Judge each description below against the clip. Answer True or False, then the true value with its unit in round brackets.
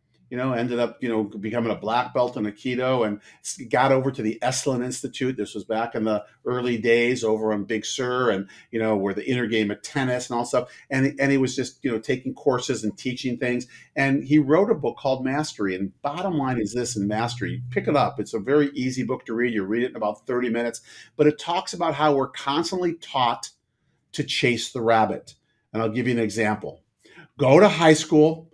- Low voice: True (125 Hz)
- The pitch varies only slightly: False (3.3 semitones)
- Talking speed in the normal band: False (225 wpm)